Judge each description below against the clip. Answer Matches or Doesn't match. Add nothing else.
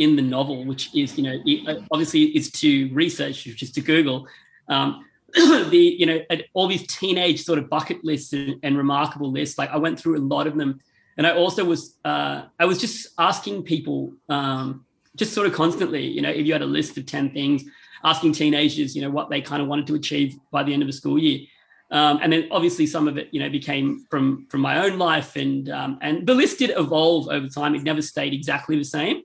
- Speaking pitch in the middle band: Matches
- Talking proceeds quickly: Matches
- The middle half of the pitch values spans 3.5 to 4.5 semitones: Doesn't match